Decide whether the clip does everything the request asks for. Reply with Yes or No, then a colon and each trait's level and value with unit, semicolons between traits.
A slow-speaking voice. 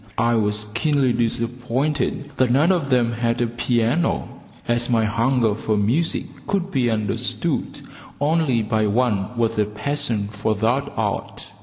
No: average, 145 wpm